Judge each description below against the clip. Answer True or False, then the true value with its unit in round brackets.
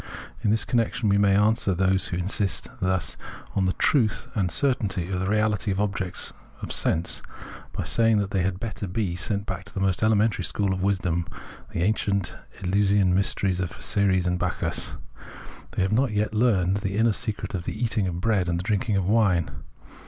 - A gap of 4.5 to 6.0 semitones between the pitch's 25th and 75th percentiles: False (2.6 semitones)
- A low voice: True (100 Hz)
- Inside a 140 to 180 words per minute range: False (190 wpm)